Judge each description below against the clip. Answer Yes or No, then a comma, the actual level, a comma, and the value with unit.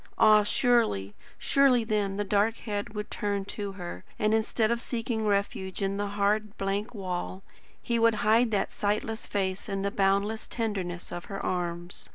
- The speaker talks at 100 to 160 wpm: No, average, 170 wpm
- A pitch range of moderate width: No, narrow, 2.1 semitones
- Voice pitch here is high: Yes, high, 205 Hz